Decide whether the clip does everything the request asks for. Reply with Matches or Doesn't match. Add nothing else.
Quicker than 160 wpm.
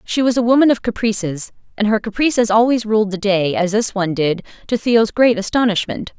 Matches